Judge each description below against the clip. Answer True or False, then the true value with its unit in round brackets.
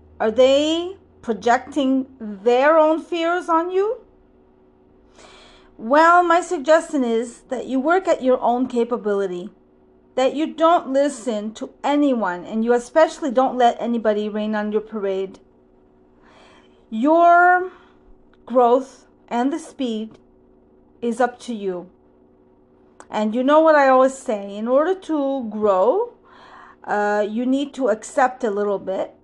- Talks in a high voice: True (255 Hz)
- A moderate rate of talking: False (130 wpm)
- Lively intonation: True (6.3 semitones)